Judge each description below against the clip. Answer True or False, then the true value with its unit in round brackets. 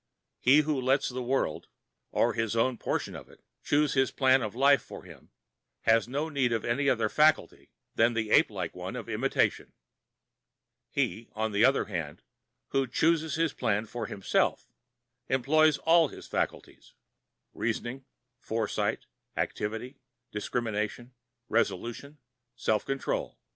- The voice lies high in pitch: False (125 Hz)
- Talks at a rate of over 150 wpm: False (135 wpm)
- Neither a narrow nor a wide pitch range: True (3.8 semitones)